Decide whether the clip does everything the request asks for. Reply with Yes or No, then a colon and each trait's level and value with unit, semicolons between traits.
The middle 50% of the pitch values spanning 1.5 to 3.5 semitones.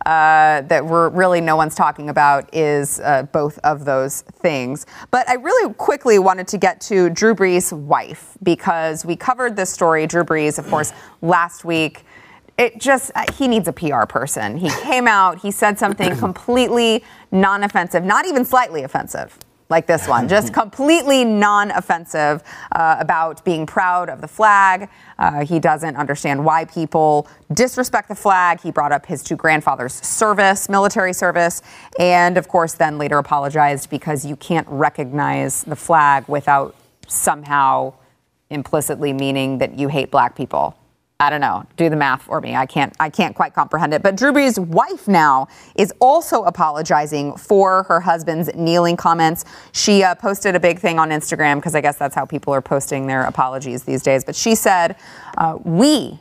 No: average, 4.8 semitones